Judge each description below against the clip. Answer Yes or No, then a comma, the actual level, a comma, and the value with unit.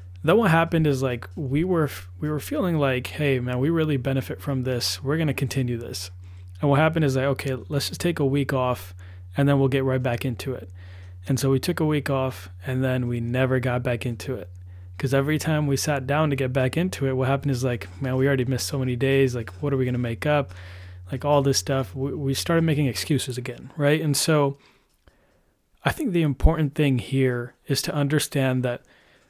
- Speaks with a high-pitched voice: No, low, 135 Hz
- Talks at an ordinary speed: No, fast, 225 wpm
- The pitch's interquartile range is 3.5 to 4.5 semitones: No, average, 2.7 semitones